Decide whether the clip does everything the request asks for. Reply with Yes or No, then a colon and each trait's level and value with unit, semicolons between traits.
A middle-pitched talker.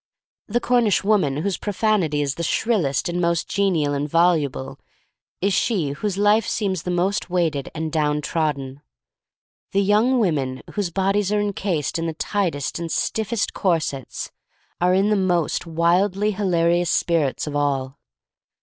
Yes: medium, 175 Hz